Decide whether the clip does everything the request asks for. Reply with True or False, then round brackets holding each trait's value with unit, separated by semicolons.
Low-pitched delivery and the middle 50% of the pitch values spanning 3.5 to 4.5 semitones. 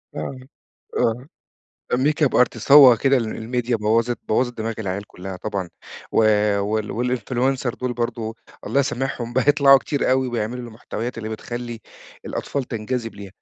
False (120 Hz; 2.8 semitones)